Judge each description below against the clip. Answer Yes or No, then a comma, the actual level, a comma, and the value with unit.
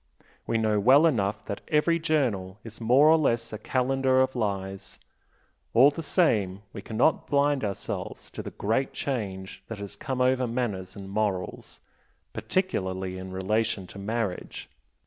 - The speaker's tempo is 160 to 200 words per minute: No, average, 150 wpm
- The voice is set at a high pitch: No, low, 115 Hz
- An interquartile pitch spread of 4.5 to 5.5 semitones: Yes, average, 5.1 semitones